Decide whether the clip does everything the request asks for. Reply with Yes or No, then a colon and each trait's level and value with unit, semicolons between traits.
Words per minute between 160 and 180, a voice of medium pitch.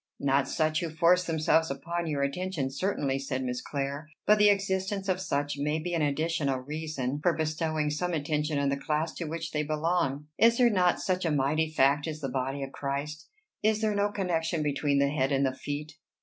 No: fast, 205 wpm; medium, 155 Hz